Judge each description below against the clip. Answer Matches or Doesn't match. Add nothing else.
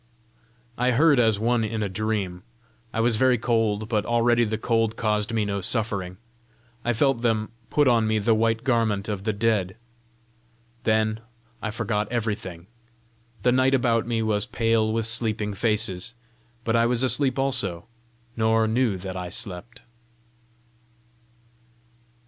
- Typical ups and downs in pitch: Doesn't match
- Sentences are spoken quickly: Doesn't match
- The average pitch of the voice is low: Matches